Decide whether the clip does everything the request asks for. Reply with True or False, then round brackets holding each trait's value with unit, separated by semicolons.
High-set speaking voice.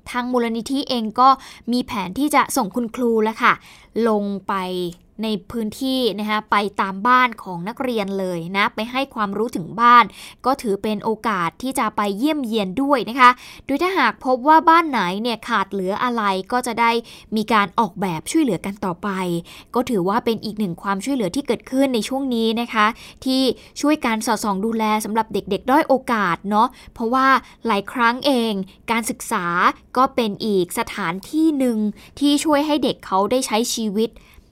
True (230 Hz)